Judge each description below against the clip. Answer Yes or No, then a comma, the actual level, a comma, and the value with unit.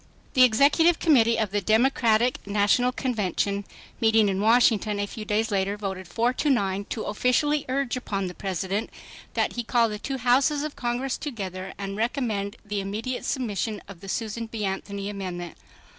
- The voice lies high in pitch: Yes, high, 220 Hz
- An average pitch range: Yes, average, 3.8 semitones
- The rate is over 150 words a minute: Yes, average, 170 wpm